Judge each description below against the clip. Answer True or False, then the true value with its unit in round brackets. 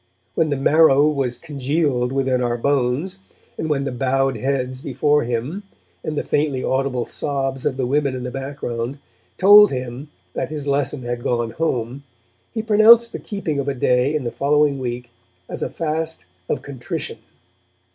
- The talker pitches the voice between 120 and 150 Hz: True (135 Hz)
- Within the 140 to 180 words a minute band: True (165 wpm)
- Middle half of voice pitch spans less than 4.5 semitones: True (3.1 semitones)